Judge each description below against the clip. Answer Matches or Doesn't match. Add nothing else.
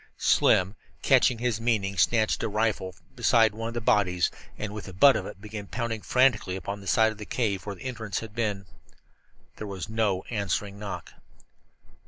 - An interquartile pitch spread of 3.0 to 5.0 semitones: Doesn't match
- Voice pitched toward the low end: Matches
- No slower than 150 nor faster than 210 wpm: Matches